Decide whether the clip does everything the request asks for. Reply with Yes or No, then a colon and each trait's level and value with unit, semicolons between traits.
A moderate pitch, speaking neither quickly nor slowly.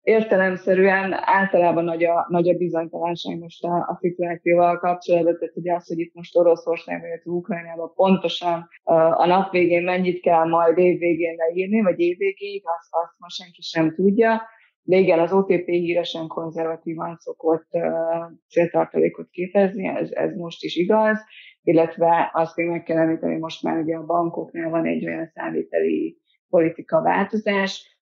Yes: medium, 170 Hz; average, 145 wpm